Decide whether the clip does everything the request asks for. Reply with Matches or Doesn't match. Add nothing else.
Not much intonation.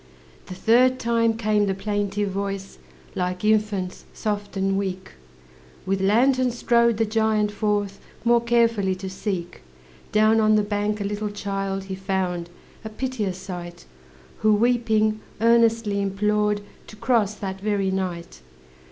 Matches